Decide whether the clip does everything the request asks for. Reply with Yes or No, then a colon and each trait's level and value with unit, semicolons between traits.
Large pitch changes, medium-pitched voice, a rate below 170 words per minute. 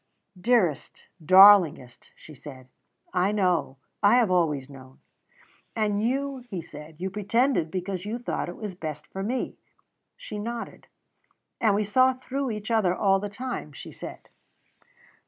No: wide, 5.7 semitones; high, 200 Hz; average, 145 wpm